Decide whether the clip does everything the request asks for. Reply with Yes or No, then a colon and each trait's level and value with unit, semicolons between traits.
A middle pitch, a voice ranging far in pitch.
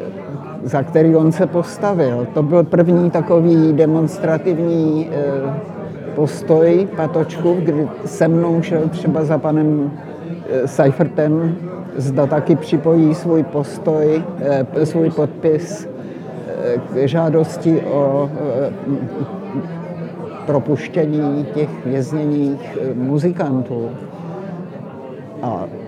No: medium, 160 Hz; average, 2.7 semitones